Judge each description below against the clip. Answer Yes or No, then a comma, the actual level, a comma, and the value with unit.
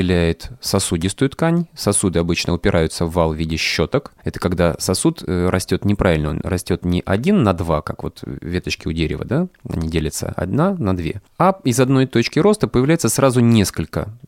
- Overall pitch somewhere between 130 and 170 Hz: No, very low, 95 Hz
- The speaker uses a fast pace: Yes, fast, 170 wpm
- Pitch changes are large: Yes, wide, 7.3 semitones